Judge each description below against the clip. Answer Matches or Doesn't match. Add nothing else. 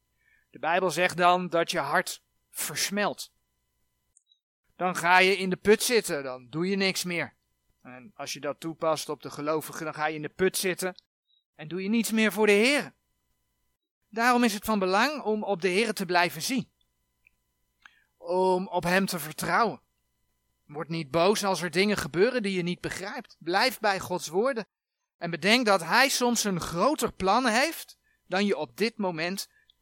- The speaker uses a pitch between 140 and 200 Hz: Matches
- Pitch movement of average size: Matches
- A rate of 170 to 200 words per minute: Matches